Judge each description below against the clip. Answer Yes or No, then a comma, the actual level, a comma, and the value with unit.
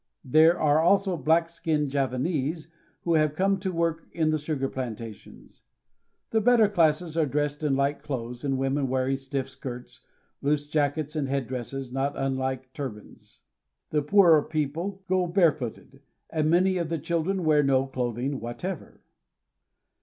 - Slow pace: No, average, 150 wpm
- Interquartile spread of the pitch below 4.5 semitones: Yes, average, 3.8 semitones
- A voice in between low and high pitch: Yes, medium, 150 Hz